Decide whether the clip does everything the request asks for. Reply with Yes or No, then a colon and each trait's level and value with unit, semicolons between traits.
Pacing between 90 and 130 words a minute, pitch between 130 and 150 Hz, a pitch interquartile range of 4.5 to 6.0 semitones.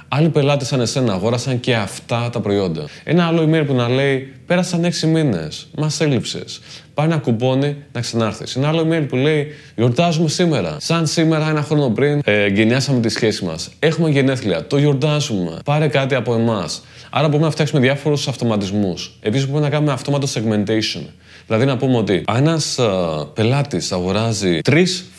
No: average, 165 wpm; low, 135 Hz; average, 5.0 semitones